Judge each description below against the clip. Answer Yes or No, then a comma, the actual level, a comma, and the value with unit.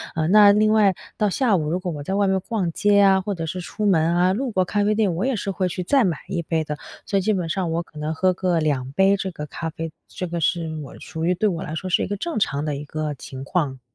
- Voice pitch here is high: No, medium, 180 Hz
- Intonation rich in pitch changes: No, average, 3.8 semitones